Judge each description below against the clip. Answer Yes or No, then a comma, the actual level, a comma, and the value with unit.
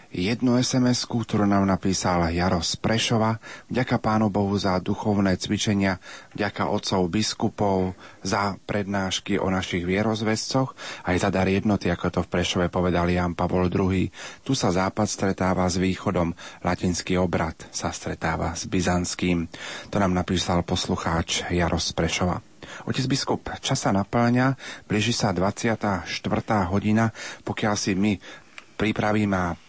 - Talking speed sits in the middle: Yes, average, 130 wpm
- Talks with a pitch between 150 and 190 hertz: No, low, 100 Hz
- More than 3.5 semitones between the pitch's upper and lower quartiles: No, average, 3.1 semitones